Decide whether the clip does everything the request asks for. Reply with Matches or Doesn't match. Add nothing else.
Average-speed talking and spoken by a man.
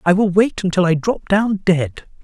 Doesn't match